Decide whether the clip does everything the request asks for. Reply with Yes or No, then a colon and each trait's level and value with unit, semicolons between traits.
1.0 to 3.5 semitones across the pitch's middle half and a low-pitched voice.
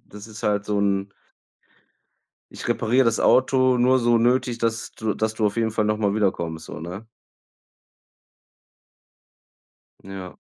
Yes: narrow, 2.6 semitones; low, 110 Hz